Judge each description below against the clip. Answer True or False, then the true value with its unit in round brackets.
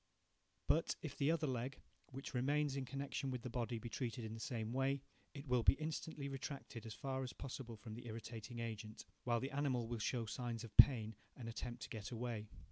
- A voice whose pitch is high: False (125 Hz)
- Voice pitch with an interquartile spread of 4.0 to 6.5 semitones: False (3.1 semitones)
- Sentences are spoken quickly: True (210 wpm)